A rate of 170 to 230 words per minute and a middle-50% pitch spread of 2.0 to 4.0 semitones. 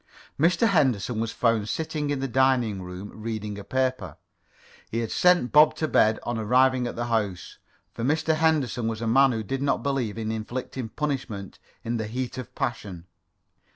Yes: average, 180 wpm; average, 3.7 semitones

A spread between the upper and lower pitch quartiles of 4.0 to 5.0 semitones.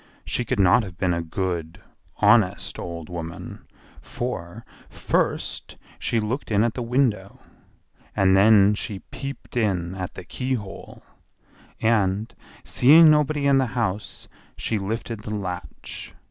Yes: average, 4.6 semitones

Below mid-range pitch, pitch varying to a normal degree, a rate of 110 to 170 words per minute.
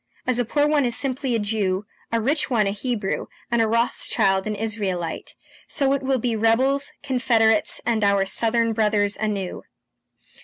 No: high, 225 Hz; average, 3.3 semitones; average, 165 wpm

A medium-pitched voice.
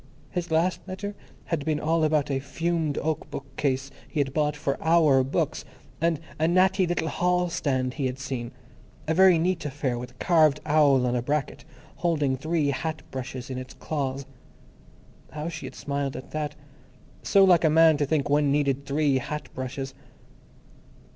Yes: medium, 150 Hz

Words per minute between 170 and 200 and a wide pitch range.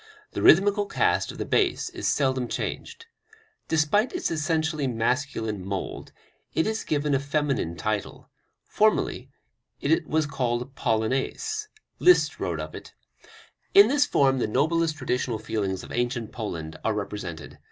No: average, 140 wpm; wide, 6.4 semitones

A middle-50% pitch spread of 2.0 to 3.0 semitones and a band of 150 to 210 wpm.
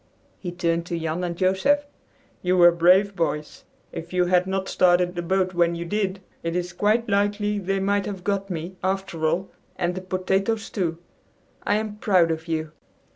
Yes: narrow, 2.4 semitones; average, 180 wpm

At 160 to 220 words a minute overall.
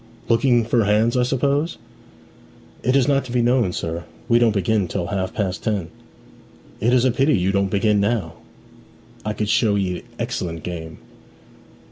Yes: average, 165 wpm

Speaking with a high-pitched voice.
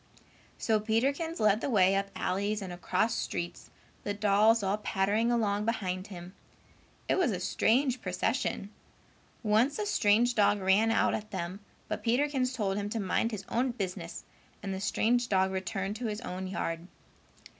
Yes: high, 210 Hz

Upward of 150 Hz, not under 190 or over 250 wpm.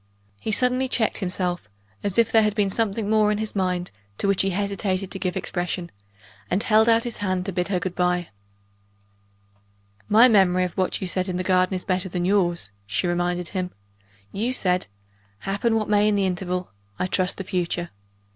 Yes: high, 190 Hz; average, 195 wpm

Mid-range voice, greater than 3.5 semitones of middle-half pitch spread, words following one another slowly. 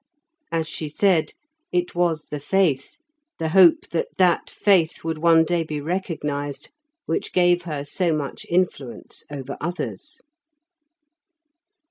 No: medium, 165 Hz; average, 2.9 semitones; slow, 125 wpm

